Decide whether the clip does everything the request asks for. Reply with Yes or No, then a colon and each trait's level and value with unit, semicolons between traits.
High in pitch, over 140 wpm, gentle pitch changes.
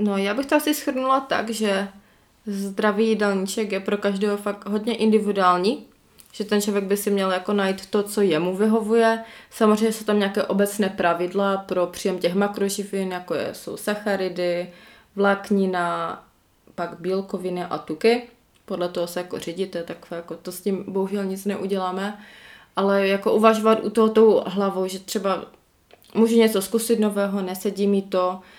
Yes: high, 200 Hz; average, 160 wpm; narrow, 2.3 semitones